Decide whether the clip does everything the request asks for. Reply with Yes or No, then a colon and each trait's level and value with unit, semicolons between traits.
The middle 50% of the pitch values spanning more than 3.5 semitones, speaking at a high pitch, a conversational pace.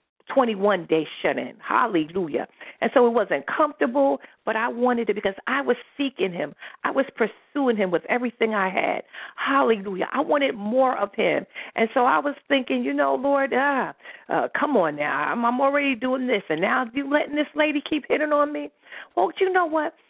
Yes: average, 4.5 semitones; very high, 255 Hz; average, 195 wpm